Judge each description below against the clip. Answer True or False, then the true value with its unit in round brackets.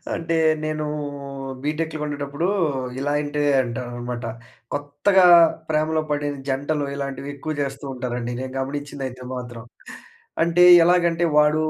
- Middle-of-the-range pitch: True (145 Hz)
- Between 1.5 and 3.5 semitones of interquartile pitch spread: True (2.7 semitones)